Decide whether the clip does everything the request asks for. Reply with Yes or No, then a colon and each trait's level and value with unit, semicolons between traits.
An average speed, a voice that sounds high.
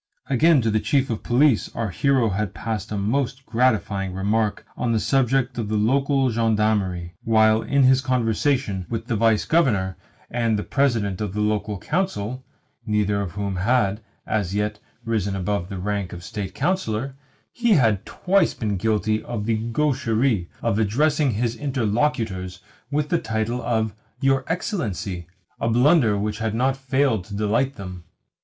No: average, 160 wpm; low, 110 Hz